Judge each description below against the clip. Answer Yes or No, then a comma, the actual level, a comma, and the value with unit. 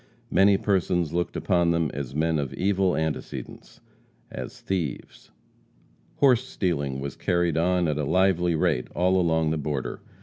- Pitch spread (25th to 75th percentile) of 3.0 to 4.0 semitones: Yes, average, 3.3 semitones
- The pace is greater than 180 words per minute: No, average, 145 wpm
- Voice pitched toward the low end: Yes, very low, 85 Hz